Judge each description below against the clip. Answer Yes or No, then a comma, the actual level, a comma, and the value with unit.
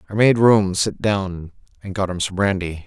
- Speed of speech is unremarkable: No, fast, 210 wpm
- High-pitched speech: No, very low, 95 Hz